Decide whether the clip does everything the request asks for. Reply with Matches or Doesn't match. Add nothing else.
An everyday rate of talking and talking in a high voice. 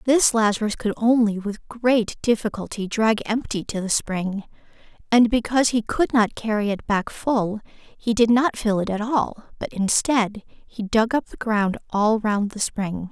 Matches